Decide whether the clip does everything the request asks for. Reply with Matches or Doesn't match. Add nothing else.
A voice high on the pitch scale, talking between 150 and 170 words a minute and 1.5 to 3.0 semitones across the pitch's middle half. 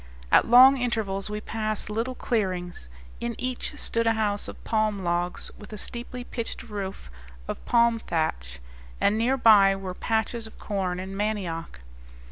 Doesn't match